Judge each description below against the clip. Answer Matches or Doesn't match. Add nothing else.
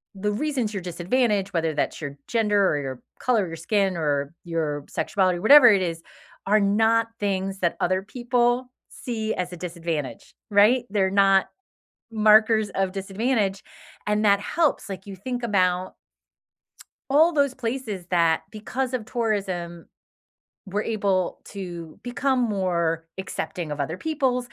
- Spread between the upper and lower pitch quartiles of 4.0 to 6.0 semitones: Matches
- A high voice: Matches